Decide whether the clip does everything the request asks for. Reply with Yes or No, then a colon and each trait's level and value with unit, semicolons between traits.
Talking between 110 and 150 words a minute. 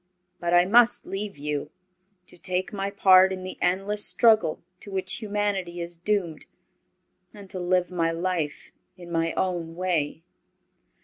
Yes: average, 145 wpm